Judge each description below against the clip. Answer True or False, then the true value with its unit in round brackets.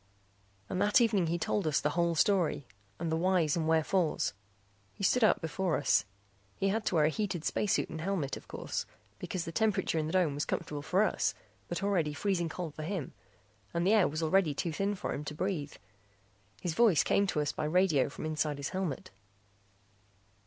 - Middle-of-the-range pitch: True (170 Hz)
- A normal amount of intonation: True (3.8 semitones)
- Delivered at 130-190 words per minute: False (200 wpm)